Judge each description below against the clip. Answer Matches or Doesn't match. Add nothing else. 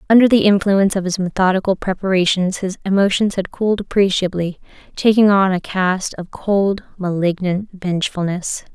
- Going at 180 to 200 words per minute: Doesn't match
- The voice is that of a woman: Matches